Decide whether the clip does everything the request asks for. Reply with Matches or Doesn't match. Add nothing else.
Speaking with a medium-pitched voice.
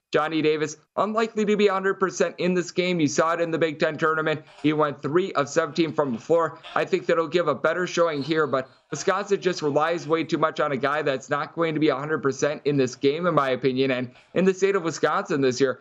Matches